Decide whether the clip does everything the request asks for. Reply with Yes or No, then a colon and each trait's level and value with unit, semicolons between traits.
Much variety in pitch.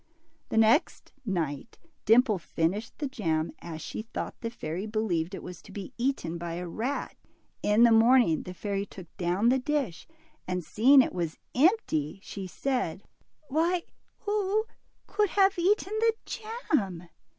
Yes: wide, 7.9 semitones